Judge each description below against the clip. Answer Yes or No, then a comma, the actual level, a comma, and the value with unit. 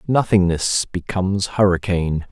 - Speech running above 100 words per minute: No, slow, 80 wpm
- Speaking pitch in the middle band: No, very low, 95 Hz